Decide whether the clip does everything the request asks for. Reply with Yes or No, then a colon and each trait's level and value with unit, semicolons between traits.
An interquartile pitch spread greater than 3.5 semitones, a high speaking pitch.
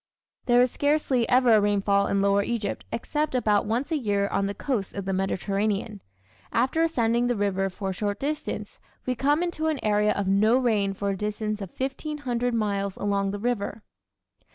Yes: average, 4.0 semitones; high, 215 Hz